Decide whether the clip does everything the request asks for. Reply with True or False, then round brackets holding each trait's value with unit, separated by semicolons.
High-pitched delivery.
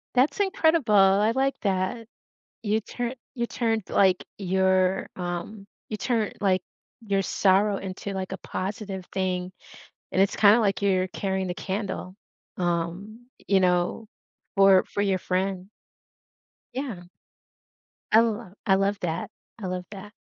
True (195 Hz)